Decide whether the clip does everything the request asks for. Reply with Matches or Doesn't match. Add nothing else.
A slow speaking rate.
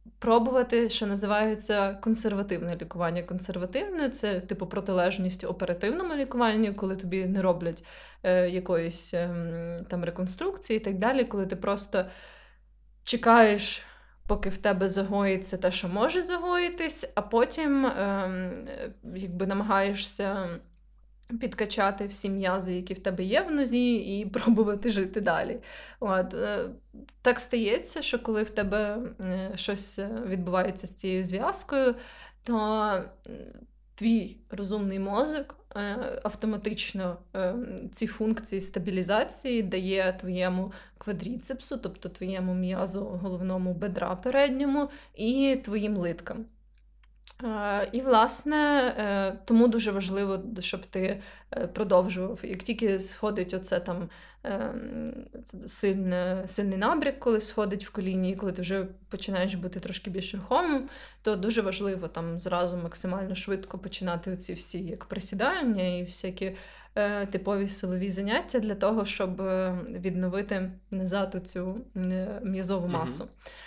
Doesn't match